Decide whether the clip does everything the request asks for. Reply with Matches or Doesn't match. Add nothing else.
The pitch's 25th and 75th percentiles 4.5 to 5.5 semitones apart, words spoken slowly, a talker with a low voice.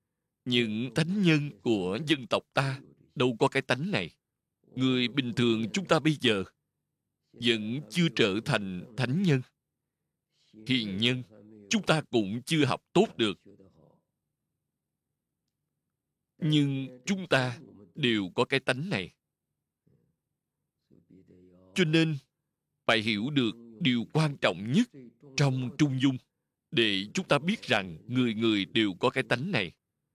Matches